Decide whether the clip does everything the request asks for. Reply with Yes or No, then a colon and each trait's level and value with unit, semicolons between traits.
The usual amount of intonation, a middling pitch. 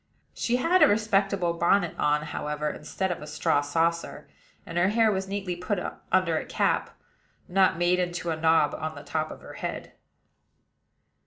Yes: average, 3.6 semitones; medium, 175 Hz